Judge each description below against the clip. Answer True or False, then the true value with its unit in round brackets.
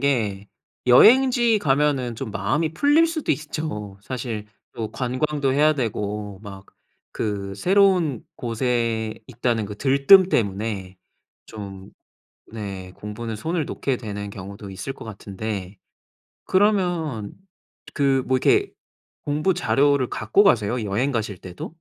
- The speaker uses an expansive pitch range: True (6.3 semitones)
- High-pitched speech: False (120 Hz)